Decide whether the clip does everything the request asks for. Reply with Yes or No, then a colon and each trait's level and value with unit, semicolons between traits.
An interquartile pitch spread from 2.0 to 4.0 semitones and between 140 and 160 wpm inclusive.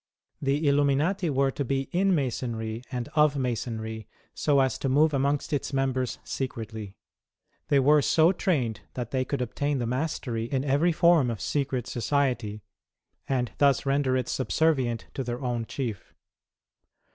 Yes: average, 3.1 semitones; average, 150 wpm